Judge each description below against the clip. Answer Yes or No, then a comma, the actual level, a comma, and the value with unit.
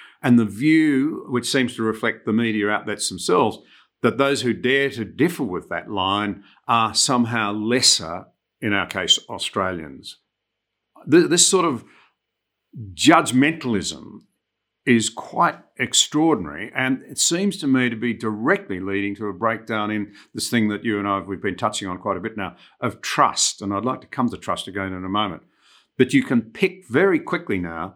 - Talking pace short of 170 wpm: No, average, 175 wpm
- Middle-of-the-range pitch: No, low, 115 Hz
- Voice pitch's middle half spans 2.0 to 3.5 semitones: No, average, 4.2 semitones